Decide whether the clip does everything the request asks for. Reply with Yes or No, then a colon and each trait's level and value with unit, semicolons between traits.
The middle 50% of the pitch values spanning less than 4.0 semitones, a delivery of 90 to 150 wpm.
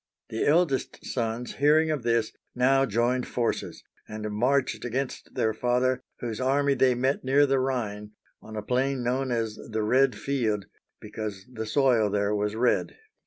No: average, 3.5 semitones; average, 165 wpm